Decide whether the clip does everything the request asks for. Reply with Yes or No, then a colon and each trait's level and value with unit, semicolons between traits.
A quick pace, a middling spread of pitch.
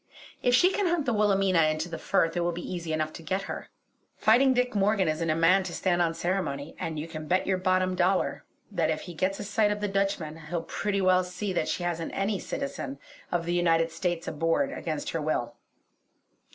Yes: fast, 220 wpm; average, 3.2 semitones